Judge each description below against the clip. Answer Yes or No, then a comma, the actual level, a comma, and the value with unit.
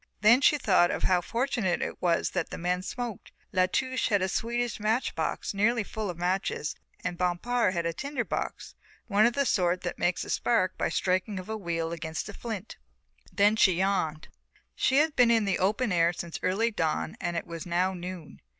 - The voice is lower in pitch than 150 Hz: No, high, 190 Hz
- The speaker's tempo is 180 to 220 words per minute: Yes, average, 200 wpm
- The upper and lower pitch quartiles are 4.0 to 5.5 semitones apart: Yes, average, 4.6 semitones